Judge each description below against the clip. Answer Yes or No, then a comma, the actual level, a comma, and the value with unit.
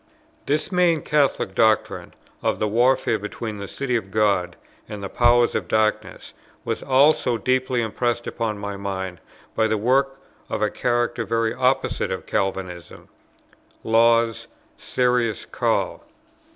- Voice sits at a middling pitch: No, low, 115 Hz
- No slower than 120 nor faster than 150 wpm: Yes, slow, 135 wpm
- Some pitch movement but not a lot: Yes, average, 3.2 semitones